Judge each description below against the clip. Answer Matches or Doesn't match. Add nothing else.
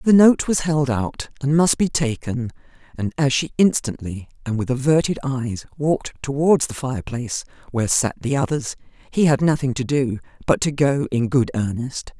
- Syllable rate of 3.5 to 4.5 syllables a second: Doesn't match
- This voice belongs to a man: Doesn't match